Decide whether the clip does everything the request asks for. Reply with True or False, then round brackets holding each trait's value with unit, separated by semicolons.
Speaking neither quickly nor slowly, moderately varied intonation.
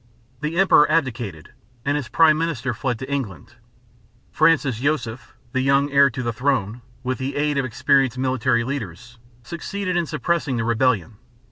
True (155 wpm; 3.7 semitones)